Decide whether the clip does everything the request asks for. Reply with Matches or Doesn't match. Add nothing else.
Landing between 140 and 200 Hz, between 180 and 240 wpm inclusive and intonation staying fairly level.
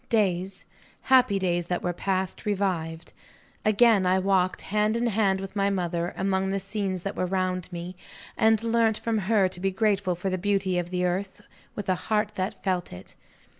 Matches